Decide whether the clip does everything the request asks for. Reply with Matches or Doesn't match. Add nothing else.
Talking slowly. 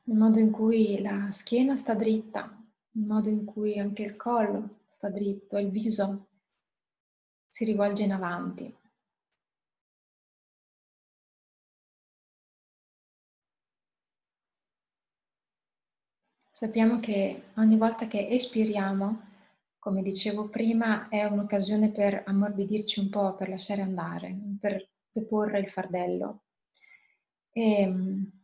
Matches